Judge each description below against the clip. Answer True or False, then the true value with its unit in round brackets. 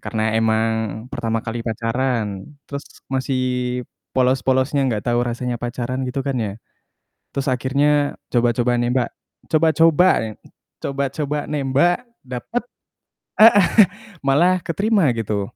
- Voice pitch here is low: True (130 Hz)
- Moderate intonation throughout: True (3.9 semitones)